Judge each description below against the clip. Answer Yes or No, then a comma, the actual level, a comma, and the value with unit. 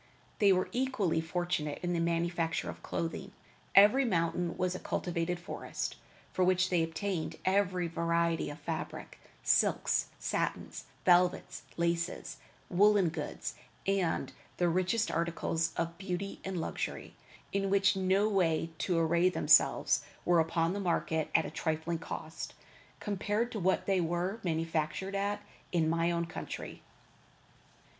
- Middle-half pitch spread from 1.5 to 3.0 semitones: Yes, narrow, 2.6 semitones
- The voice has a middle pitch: Yes, medium, 175 Hz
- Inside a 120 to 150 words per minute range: Yes, slow, 135 wpm